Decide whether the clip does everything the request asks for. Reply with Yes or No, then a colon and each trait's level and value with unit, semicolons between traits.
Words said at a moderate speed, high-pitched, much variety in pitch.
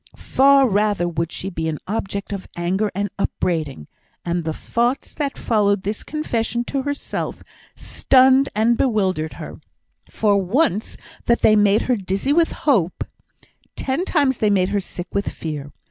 Yes: average, 160 wpm; high, 205 Hz; wide, 5.8 semitones